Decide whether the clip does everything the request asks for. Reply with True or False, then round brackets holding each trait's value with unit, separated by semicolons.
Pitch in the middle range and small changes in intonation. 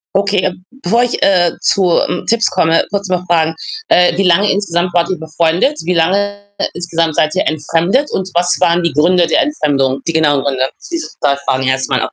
False (175 Hz; 3.2 semitones)